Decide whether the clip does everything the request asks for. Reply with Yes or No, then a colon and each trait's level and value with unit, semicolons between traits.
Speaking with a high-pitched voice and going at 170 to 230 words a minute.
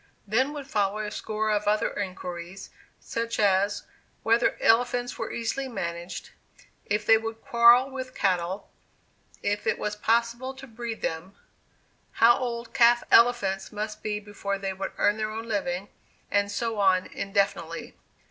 No: high, 215 Hz; average, 145 wpm